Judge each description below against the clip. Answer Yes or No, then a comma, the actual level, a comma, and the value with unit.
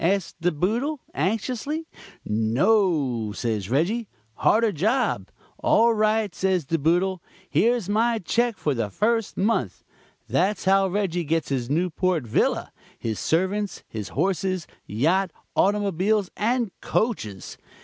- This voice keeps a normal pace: No, slow, 120 wpm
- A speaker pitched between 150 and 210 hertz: Yes, high, 190 Hz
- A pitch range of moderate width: No, wide, 6.0 semitones